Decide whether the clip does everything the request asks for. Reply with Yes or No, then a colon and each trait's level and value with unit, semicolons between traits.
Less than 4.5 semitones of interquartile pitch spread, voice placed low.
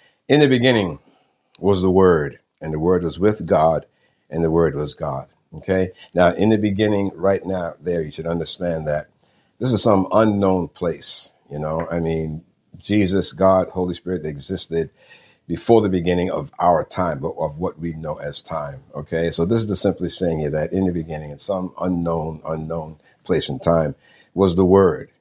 Yes: average, 3.0 semitones; very low, 90 Hz